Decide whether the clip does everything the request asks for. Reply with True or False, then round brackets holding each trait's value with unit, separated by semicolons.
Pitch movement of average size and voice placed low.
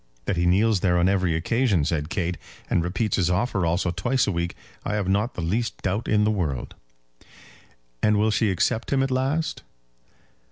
True (4.2 semitones; 95 Hz)